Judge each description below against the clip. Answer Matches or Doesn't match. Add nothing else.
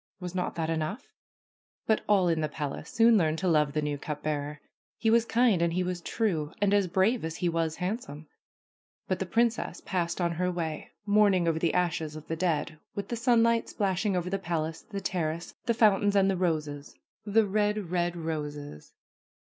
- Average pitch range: Matches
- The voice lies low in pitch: Doesn't match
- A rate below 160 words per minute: Doesn't match